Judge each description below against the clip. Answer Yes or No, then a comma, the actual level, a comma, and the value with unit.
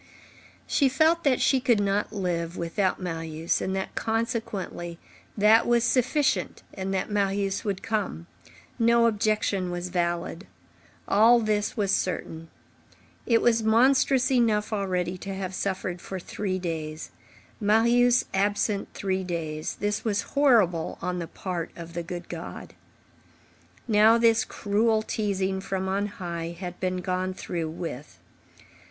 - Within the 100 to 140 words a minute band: Yes, slow, 135 wpm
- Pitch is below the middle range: No, high, 195 Hz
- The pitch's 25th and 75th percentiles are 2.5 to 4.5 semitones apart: Yes, average, 3.9 semitones